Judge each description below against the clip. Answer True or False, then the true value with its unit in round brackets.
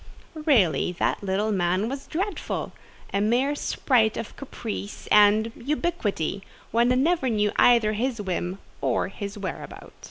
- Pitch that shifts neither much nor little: True (4.8 semitones)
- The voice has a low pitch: False (220 Hz)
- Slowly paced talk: True (130 wpm)